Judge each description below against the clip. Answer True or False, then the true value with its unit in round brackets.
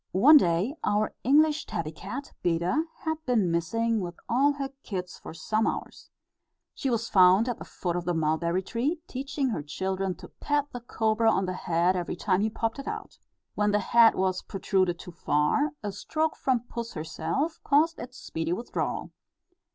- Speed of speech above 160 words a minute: True (180 wpm)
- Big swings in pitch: True (6.3 semitones)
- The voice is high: True (210 Hz)